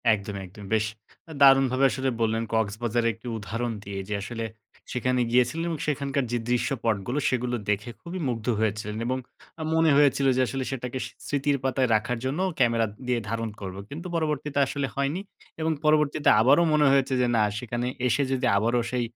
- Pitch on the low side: Yes, low, 125 Hz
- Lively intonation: No, average, 3.6 semitones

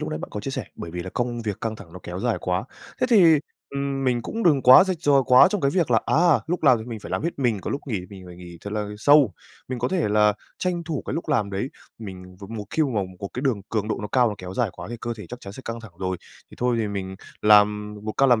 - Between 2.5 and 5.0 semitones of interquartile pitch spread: No, wide, 5.4 semitones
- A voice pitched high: No, low, 115 Hz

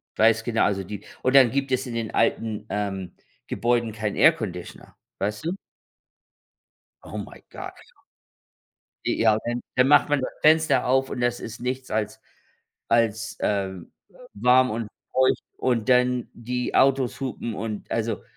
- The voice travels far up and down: No, average, 2.9 semitones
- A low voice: Yes, low, 120 Hz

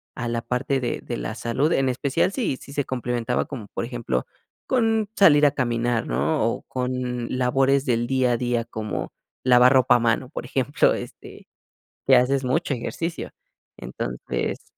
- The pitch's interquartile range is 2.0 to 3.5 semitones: Yes, narrow, 2.4 semitones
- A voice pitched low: Yes, low, 125 Hz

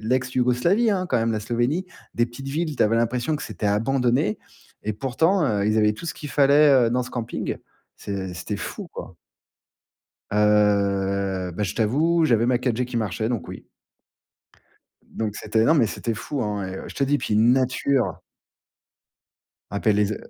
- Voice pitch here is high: No, low, 120 Hz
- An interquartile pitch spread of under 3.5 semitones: No, average, 4.5 semitones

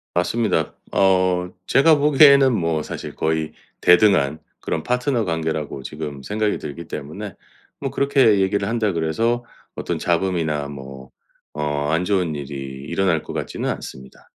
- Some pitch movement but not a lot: No, wide, 5.9 semitones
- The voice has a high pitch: No, very low, 90 Hz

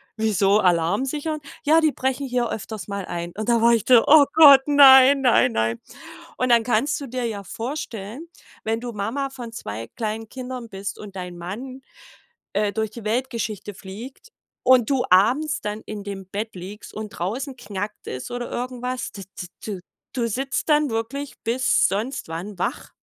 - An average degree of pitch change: Yes, average, 4.4 semitones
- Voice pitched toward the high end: Yes, high, 230 Hz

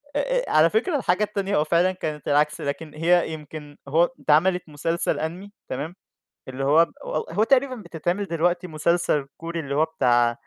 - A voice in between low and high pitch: Yes, medium, 165 Hz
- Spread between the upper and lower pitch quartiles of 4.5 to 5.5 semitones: No, average, 3.3 semitones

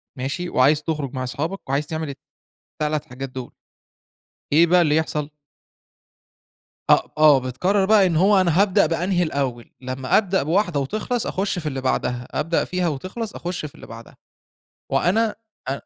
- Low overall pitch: No, medium, 155 Hz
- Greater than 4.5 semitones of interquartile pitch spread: Yes, average, 5.2 semitones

